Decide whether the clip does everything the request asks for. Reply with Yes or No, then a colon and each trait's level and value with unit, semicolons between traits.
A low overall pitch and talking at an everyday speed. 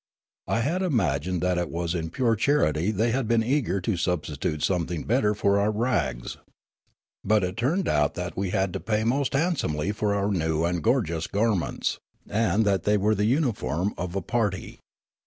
Yes: low, 100 Hz; average, 190 wpm